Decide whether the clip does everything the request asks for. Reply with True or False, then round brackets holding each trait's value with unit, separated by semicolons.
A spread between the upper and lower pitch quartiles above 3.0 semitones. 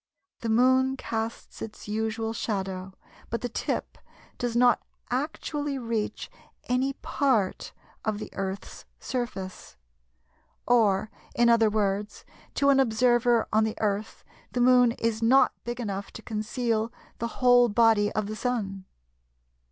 False (2.6 semitones)